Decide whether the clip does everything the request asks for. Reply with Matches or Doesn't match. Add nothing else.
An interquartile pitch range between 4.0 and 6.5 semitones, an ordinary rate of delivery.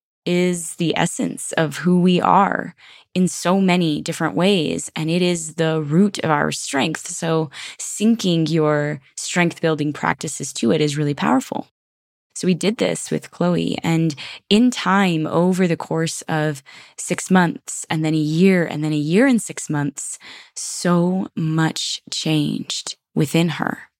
Doesn't match